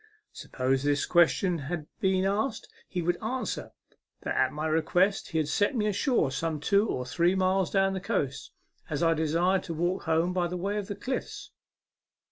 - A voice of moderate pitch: Yes, medium, 175 Hz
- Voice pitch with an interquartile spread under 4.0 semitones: Yes, average, 3.4 semitones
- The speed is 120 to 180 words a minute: Yes, average, 175 wpm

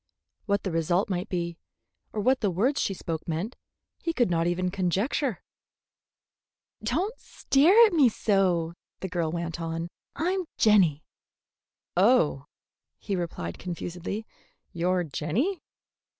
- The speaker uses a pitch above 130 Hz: Yes, medium, 185 Hz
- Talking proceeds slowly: Yes, slow, 125 wpm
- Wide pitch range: Yes, wide, 6.0 semitones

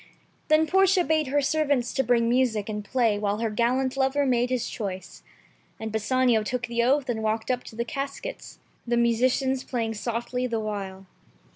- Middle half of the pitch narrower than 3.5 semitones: Yes, average, 3.1 semitones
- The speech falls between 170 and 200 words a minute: Yes, average, 180 wpm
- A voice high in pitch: Yes, high, 245 Hz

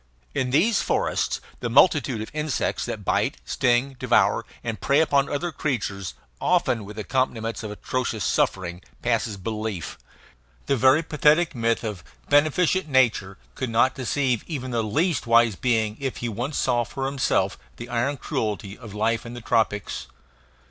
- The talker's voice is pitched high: No, low, 120 Hz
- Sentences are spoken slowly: No, average, 155 wpm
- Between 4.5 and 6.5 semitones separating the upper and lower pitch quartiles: No, average, 4.0 semitones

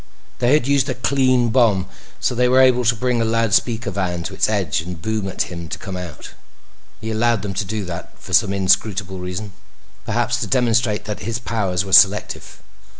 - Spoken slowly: No, average, 200 wpm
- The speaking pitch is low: Yes, low, 110 Hz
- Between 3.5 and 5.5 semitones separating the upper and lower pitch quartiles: Yes, average, 3.9 semitones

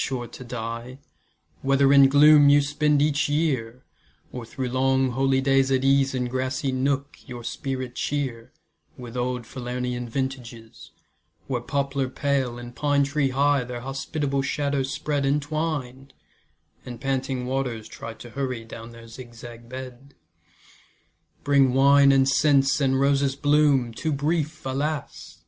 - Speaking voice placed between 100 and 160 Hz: Yes, low, 135 Hz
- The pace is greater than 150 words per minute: No, slow, 135 wpm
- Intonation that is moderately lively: No, narrow, 2.2 semitones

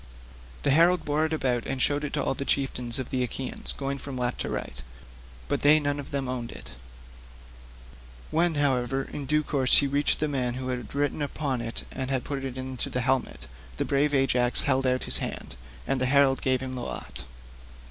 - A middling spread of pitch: No, narrow, 2.1 semitones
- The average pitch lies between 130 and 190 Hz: Yes, low, 135 Hz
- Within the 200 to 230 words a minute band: Yes, fast, 205 wpm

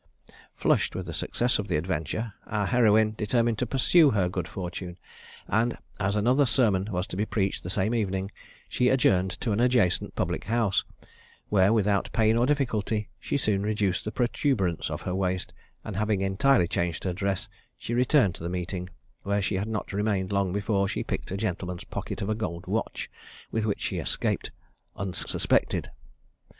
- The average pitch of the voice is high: No, low, 100 Hz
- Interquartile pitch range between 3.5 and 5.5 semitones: No, average, 3.1 semitones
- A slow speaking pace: No, average, 180 wpm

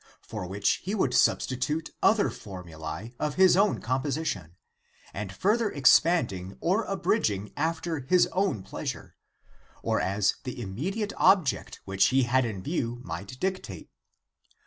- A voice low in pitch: Yes, low, 130 Hz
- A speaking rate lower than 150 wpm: Yes, slow, 135 wpm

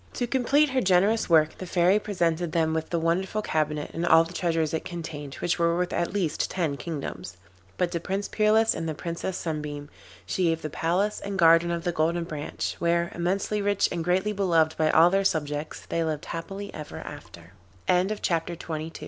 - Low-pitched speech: No, medium, 170 Hz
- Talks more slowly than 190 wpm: No, average, 195 wpm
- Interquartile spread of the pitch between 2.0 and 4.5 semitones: Yes, average, 3.0 semitones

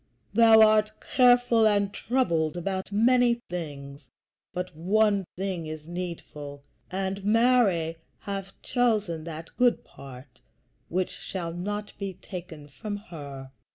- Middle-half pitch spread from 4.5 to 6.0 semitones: Yes, average, 5.0 semitones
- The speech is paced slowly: Yes, slow, 120 wpm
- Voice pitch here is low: No, high, 190 Hz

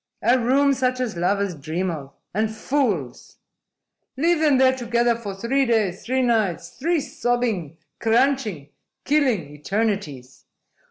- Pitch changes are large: Yes, wide, 6.2 semitones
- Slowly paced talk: Yes, slow, 125 wpm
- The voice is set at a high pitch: Yes, high, 230 Hz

